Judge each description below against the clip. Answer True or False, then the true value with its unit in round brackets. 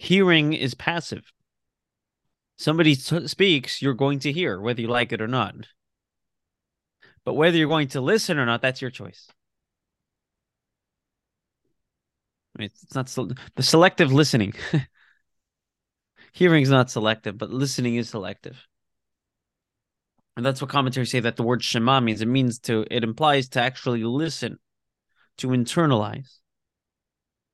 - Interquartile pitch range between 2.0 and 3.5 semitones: False (4.3 semitones)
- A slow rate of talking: True (130 wpm)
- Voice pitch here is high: False (130 Hz)